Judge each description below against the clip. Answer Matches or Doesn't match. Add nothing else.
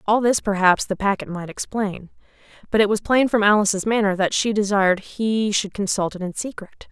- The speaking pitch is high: Matches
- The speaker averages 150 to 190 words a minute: Doesn't match